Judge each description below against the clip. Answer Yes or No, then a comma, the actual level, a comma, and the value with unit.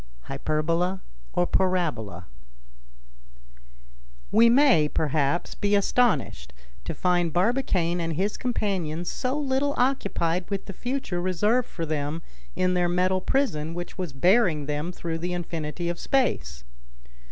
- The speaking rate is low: Yes, slow, 125 wpm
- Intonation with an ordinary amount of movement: Yes, average, 4.3 semitones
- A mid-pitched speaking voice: Yes, medium, 175 Hz